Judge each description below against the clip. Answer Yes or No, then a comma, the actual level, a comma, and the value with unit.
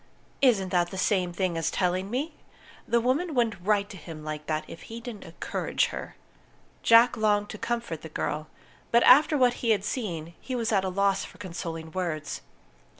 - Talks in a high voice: Yes, high, 195 Hz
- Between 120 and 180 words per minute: No, average, 190 wpm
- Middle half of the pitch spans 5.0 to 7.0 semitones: Yes, average, 5.3 semitones